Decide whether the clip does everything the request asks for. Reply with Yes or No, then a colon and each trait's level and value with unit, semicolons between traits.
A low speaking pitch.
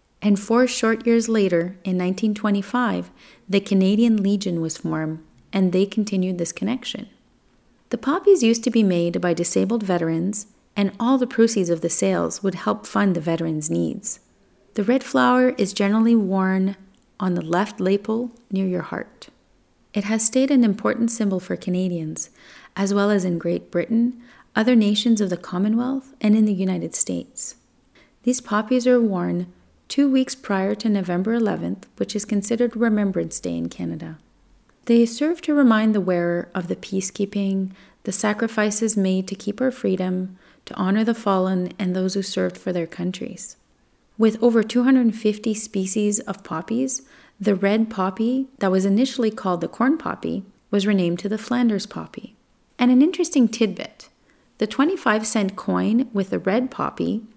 No: high, 210 Hz